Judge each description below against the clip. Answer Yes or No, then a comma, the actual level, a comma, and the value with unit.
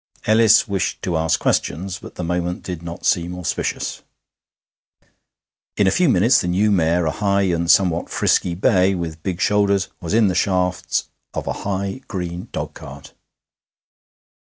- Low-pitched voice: Yes, very low, 90 Hz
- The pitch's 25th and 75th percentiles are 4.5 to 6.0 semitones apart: No, narrow, 2.5 semitones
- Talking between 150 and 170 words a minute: Yes, average, 155 wpm